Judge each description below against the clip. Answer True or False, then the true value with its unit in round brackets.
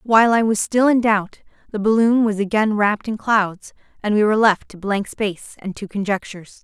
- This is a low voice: False (210 Hz)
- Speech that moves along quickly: True (210 wpm)